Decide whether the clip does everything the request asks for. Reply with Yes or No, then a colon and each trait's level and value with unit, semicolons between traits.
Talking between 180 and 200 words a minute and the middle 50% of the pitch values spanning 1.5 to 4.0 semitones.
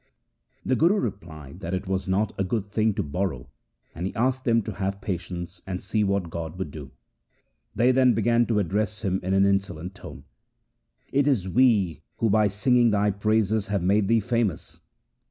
Yes: average, 190 wpm; average, 3.3 semitones